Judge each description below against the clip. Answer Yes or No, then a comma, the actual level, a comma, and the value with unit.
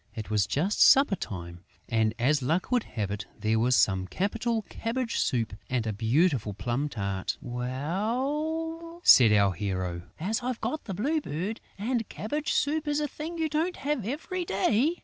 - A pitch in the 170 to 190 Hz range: Yes, medium, 185 Hz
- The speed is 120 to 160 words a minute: No, average, 170 wpm